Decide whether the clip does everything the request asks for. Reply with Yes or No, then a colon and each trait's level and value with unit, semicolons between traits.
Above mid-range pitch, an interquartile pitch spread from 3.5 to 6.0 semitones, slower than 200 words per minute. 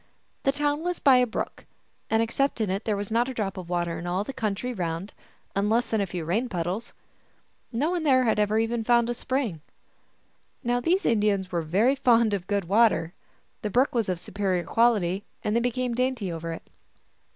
No: high, 220 Hz; average, 4.6 semitones; fast, 205 wpm